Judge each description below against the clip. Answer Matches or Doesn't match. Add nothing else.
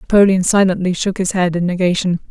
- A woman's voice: Matches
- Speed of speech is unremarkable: Matches